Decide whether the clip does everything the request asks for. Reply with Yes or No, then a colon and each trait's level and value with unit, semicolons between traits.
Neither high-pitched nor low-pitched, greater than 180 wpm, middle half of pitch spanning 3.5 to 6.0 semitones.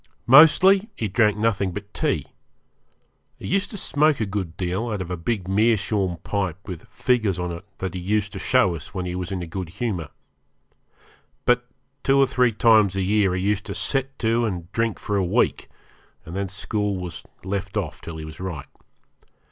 No: low, 100 Hz; average, 195 wpm; average, 4.0 semitones